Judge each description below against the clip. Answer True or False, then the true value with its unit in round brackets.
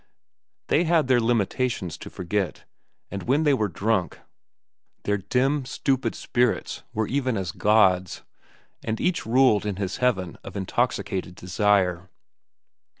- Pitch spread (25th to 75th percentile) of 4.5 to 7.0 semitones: True (5.2 semitones)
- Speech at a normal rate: False (130 wpm)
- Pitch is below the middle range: True (105 Hz)